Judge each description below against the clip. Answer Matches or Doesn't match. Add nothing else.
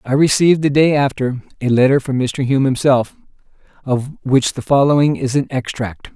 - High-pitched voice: Doesn't match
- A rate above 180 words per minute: Doesn't match